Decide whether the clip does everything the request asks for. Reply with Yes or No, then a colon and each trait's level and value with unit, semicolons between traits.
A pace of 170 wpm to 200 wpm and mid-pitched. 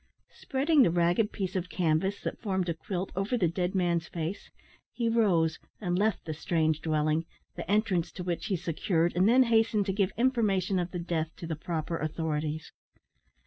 Yes: average, 185 wpm; medium, 180 Hz